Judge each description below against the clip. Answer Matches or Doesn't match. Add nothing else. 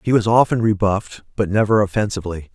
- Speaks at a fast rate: Doesn't match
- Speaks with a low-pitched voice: Matches